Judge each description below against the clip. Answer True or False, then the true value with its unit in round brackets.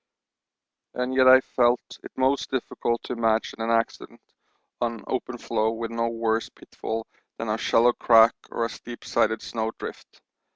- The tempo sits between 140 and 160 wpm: True (155 wpm)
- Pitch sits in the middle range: False (115 Hz)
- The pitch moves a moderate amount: False (1.5 semitones)